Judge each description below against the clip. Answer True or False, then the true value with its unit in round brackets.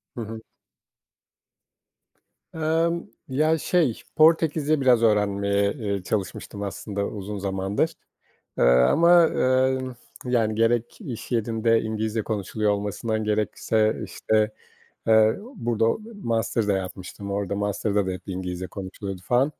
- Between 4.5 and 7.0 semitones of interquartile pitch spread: False (3.5 semitones)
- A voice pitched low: True (110 Hz)